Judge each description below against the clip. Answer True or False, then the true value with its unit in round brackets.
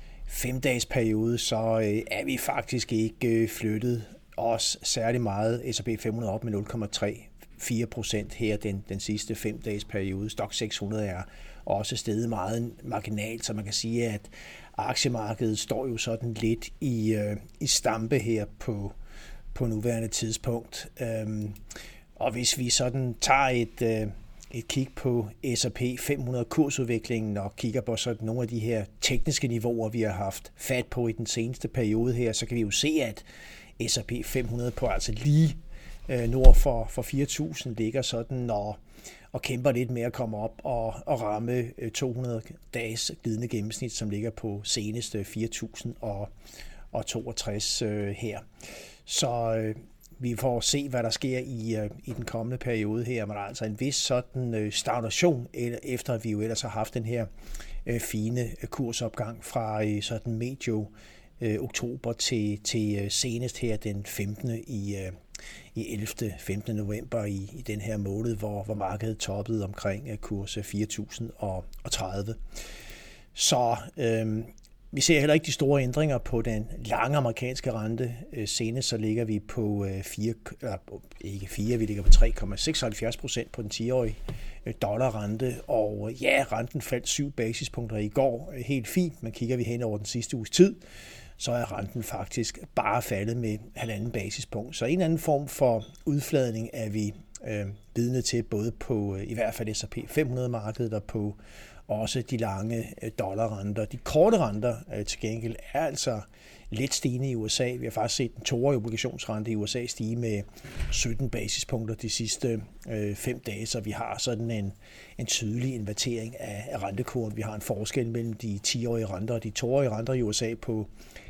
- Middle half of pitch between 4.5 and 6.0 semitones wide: False (2.4 semitones)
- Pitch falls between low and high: False (115 Hz)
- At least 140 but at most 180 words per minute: True (160 wpm)